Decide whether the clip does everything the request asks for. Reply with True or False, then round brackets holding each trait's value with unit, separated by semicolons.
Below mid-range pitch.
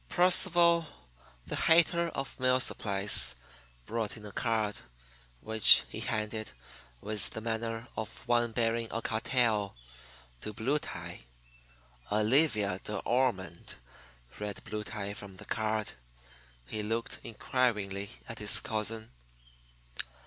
True (110 Hz)